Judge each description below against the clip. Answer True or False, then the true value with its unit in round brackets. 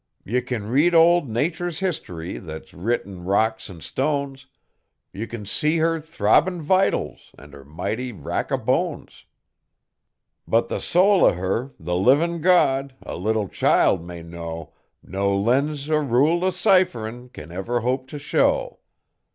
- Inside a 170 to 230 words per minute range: False (150 wpm)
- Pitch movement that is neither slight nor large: False (8.7 semitones)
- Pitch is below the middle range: True (125 Hz)